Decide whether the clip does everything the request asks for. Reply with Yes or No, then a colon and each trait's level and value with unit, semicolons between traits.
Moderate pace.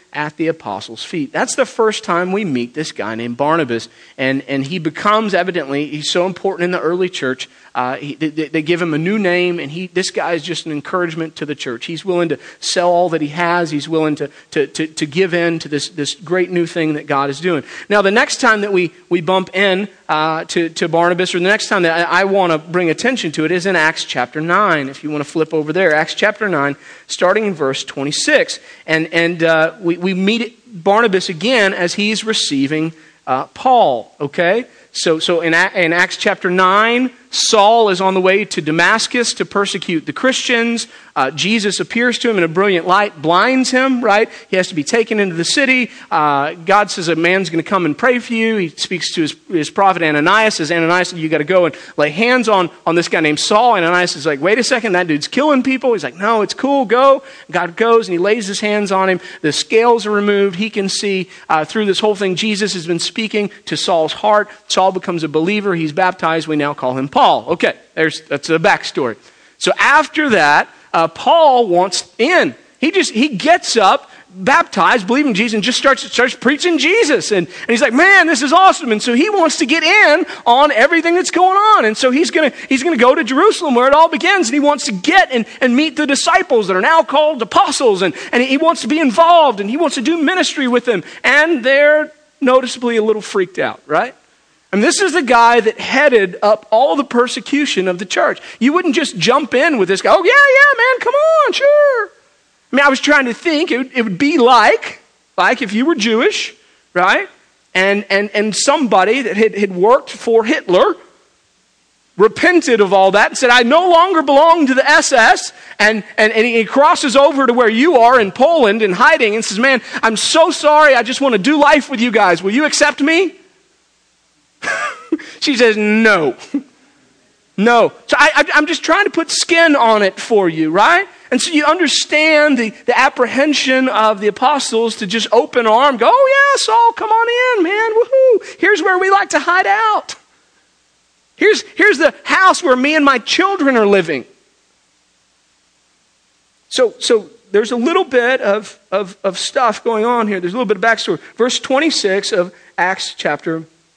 No: fast, 210 wpm